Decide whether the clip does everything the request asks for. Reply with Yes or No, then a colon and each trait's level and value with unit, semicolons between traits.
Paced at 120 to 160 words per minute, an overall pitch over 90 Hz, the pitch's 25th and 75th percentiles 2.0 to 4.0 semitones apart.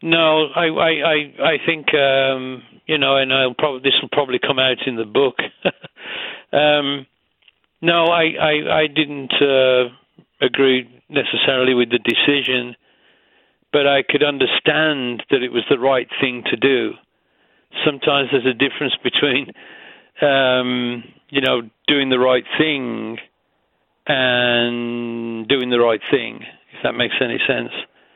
Yes: average, 140 wpm; low, 135 Hz; average, 3.0 semitones